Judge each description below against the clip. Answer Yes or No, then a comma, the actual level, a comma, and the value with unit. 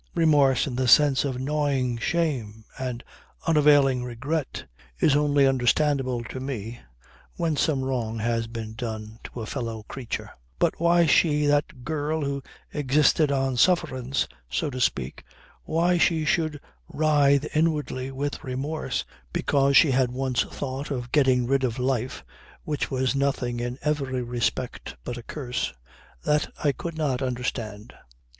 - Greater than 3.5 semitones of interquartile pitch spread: No, average, 3.2 semitones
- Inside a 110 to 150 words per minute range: Yes, average, 145 wpm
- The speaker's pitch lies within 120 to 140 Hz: Yes, low, 135 Hz